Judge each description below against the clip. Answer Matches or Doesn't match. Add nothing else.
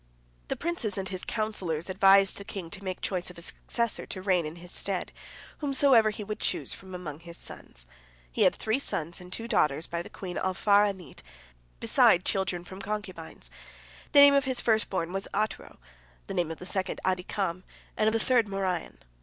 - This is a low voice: Doesn't match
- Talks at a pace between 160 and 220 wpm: Matches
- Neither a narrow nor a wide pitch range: Matches